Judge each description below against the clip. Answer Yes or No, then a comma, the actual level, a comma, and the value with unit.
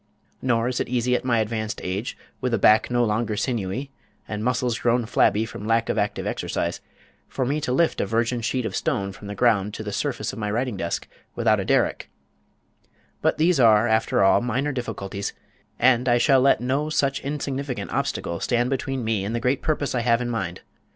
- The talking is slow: No, fast, 205 wpm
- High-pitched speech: No, low, 120 Hz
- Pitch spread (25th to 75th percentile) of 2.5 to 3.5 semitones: Yes, average, 3.0 semitones